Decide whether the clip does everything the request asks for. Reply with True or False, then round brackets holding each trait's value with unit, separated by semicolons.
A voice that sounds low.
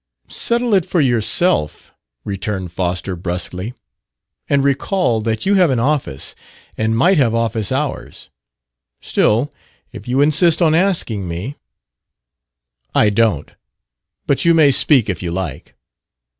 True (115 Hz)